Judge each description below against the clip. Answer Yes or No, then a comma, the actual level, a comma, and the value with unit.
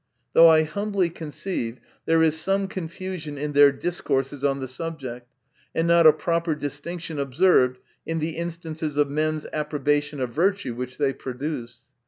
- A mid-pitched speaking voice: Yes, medium, 155 Hz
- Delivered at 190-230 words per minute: No, average, 155 wpm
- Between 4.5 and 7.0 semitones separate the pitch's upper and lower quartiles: No, average, 3.2 semitones